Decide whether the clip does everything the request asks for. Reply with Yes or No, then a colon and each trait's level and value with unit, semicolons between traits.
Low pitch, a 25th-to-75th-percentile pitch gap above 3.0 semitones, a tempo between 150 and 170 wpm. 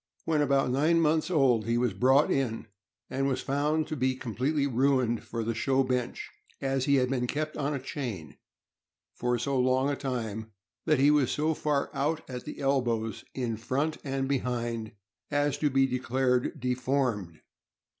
No: low, 130 Hz; narrow, 2.6 semitones; average, 165 wpm